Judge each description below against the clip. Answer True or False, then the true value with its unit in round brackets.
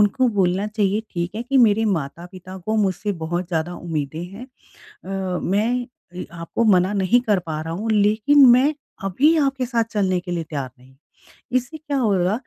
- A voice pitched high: True (200 Hz)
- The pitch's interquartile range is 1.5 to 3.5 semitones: False (4.9 semitones)